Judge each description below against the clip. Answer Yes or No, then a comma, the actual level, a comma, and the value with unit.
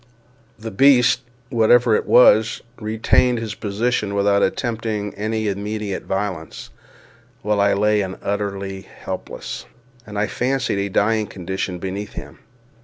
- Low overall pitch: Yes, low, 105 Hz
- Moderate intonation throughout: No, narrow, 2.0 semitones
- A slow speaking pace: Yes, slow, 130 wpm